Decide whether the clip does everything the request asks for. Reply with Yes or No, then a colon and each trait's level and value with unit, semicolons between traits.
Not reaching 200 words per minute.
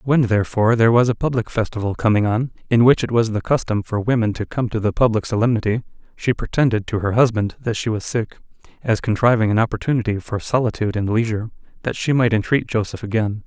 No: fast, 205 wpm